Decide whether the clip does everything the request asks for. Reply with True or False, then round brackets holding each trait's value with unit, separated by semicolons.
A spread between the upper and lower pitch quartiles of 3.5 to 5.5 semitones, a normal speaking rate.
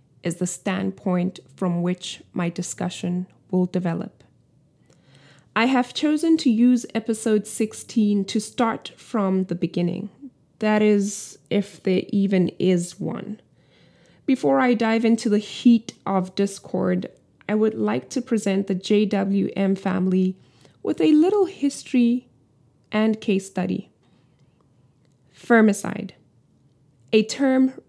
False (3.9 semitones; 115 wpm)